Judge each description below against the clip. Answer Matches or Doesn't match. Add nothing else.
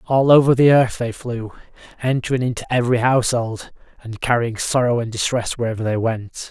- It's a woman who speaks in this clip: Doesn't match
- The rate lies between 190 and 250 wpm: Doesn't match